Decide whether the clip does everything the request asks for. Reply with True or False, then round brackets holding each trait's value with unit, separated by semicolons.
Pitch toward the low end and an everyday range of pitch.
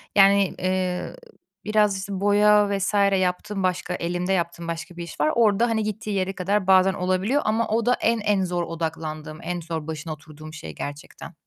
False (185 Hz; 3.5 semitones)